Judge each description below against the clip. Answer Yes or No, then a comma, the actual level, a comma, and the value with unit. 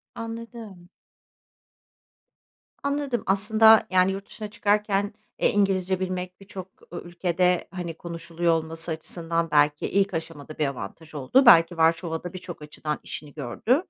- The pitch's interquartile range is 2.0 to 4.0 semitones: Yes, average, 3.7 semitones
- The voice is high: No, medium, 180 Hz